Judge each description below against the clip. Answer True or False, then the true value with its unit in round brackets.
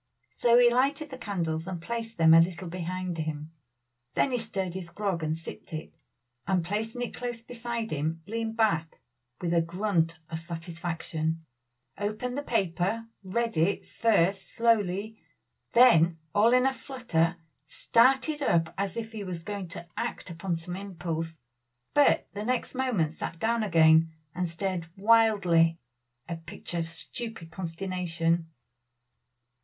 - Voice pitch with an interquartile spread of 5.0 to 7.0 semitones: True (5.5 semitones)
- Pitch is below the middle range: False (185 Hz)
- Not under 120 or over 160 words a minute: True (145 wpm)